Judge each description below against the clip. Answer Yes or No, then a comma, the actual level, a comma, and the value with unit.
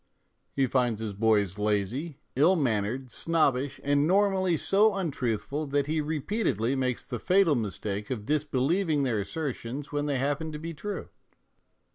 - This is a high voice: No, medium, 140 Hz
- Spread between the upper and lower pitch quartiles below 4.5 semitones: No, wide, 5.4 semitones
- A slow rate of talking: No, average, 145 wpm